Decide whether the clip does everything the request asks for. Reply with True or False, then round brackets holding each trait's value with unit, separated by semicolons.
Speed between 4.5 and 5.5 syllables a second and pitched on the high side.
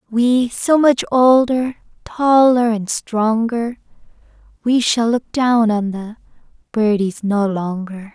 False (3.4 syllables/s; 230 Hz)